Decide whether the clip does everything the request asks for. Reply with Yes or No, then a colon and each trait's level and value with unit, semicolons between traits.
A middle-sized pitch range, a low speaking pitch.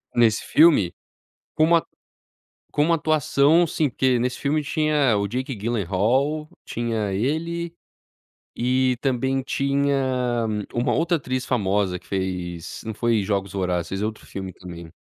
No: wide, 6.0 semitones; low, 125 Hz